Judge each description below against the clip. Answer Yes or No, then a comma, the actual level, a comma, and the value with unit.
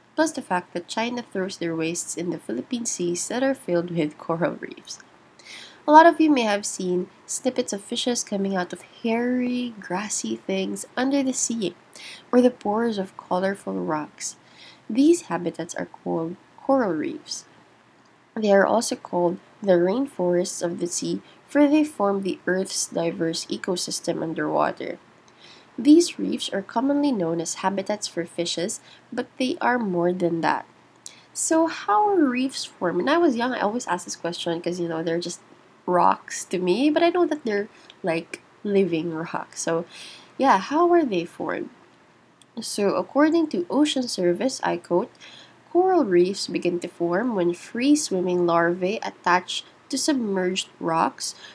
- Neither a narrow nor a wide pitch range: No, wide, 6.9 semitones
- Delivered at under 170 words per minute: Yes, average, 160 wpm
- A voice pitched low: No, high, 195 Hz